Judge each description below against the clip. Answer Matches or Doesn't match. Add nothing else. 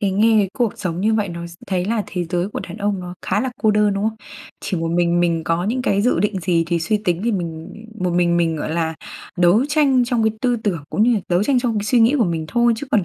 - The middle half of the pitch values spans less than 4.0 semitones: Doesn't match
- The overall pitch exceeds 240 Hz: Doesn't match